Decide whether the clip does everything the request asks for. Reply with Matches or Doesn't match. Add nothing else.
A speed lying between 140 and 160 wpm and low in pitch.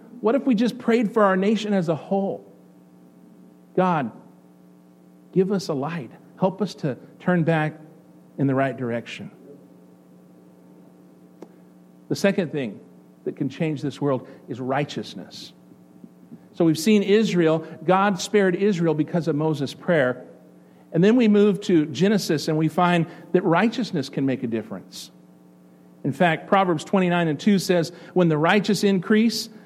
Doesn't match